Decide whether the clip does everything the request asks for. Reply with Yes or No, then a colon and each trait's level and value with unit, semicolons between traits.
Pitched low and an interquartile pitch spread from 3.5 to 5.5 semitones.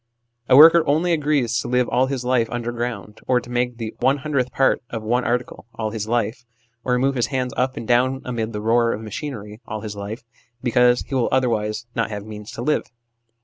No: low, 120 Hz; narrow, 2.5 semitones